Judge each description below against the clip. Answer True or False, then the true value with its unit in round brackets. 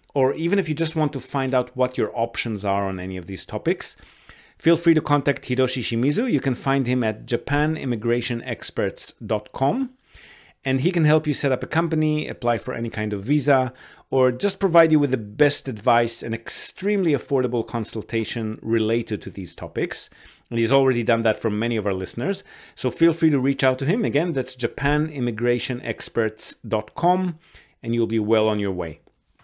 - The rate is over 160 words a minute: True (180 wpm)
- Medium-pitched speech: False (125 Hz)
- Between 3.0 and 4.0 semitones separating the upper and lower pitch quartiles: False (4.5 semitones)